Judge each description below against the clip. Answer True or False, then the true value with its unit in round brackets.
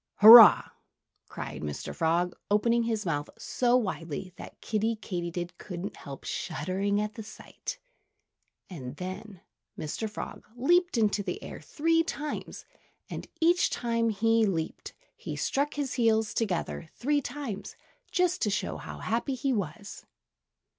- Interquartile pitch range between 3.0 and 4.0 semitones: False (5.2 semitones)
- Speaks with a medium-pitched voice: False (215 Hz)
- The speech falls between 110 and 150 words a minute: True (140 wpm)